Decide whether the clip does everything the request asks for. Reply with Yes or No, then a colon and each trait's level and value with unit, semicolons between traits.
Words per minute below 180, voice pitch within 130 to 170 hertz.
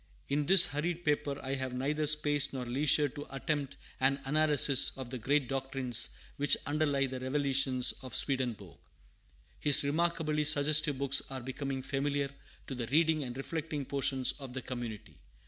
Yes: average, 155 wpm; medium, 140 Hz